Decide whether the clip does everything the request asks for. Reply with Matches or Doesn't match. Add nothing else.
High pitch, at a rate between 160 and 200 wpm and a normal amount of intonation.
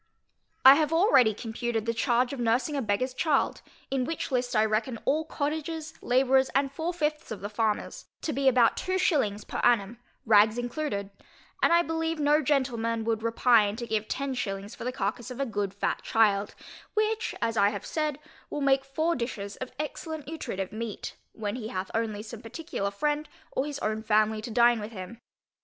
Matches